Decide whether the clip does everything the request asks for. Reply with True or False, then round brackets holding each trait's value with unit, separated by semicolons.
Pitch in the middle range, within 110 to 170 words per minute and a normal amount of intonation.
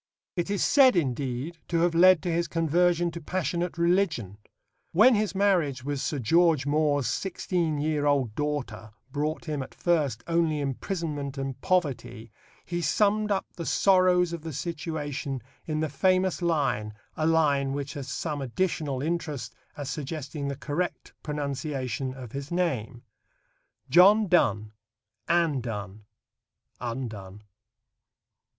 True (150 Hz; 135 wpm; 4.3 semitones)